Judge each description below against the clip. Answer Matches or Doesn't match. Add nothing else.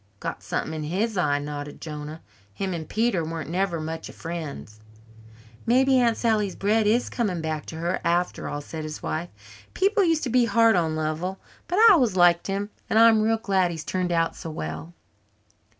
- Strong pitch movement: Matches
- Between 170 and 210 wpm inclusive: Matches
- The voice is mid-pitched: Matches